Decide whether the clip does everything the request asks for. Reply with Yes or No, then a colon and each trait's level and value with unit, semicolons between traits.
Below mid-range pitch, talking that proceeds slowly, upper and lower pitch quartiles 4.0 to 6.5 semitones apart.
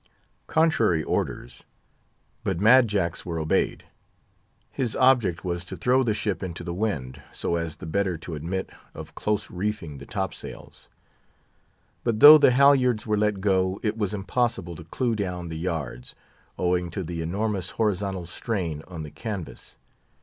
No: very low, 95 Hz; average, 155 wpm; average, 4.3 semitones